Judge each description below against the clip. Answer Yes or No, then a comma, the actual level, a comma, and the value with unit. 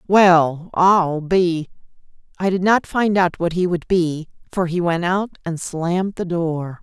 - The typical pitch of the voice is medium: Yes, medium, 175 Hz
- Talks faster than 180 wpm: No, average, 175 wpm